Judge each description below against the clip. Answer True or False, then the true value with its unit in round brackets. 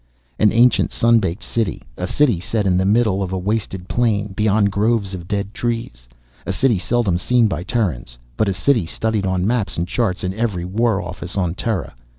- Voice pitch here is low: True (100 Hz)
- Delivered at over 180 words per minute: True (195 wpm)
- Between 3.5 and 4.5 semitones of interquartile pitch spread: True (3.8 semitones)